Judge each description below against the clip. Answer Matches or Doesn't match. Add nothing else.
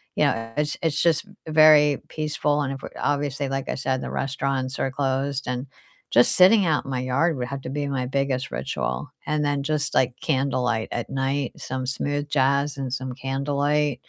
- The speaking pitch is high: Doesn't match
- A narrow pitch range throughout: Matches